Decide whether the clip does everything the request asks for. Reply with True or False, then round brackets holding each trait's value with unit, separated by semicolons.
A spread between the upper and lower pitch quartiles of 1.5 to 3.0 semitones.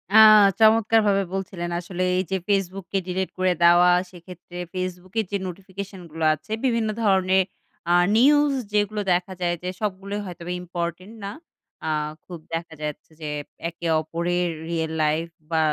True (2.4 semitones)